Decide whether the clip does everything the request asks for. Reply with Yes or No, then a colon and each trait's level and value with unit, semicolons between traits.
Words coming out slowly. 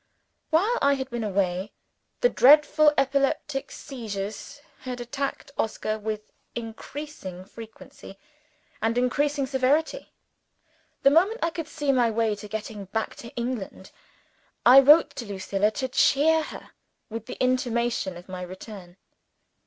Yes: slow, 130 wpm